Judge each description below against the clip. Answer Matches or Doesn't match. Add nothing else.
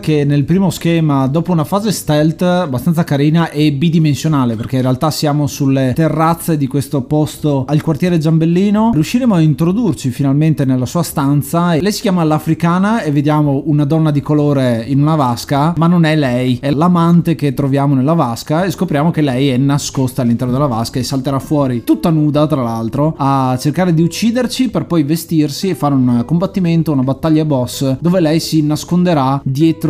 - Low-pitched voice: Doesn't match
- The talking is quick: Matches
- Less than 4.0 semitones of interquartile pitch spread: Matches